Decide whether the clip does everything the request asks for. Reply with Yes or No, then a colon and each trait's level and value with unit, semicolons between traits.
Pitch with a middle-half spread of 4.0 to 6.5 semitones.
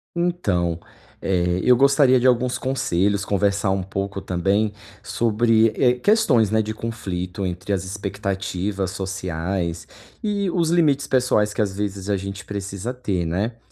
Yes: average, 4.4 semitones